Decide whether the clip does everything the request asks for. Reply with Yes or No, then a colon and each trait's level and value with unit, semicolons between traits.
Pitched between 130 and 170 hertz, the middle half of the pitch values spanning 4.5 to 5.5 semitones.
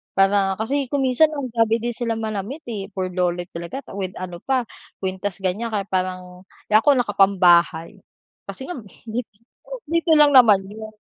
No: high, 205 Hz; average, 4.8 semitones